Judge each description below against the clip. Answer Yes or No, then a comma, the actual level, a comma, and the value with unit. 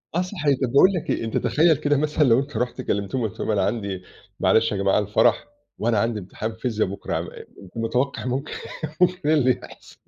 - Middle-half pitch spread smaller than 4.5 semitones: No, average, 5.2 semitones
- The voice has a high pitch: No, low, 125 Hz